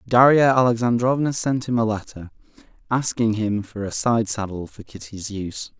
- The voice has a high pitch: No, low, 110 Hz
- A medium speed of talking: Yes, average, 155 wpm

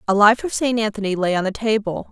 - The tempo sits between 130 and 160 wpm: No, fast, 255 wpm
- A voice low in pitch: No, high, 210 Hz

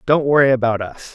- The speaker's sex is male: Yes, male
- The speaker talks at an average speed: No, fast, 210 wpm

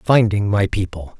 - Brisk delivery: No, average, 150 wpm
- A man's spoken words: Yes, male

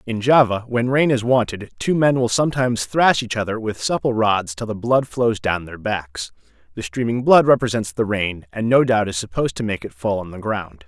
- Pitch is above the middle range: No, low, 110 Hz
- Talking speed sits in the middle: No, fast, 225 wpm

